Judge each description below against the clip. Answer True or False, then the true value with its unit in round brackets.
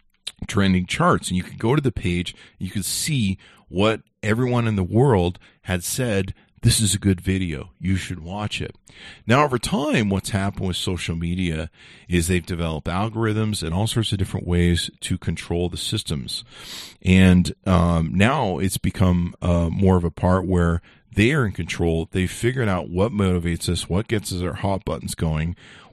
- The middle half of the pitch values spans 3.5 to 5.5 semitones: False (3.1 semitones)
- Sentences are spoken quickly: False (190 wpm)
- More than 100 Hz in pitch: False (95 Hz)